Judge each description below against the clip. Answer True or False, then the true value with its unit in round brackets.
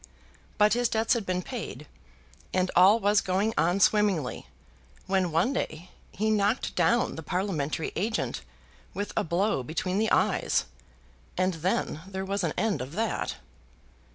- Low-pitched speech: False (190 Hz)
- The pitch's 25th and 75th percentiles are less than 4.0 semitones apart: True (3.3 semitones)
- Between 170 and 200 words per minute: False (150 wpm)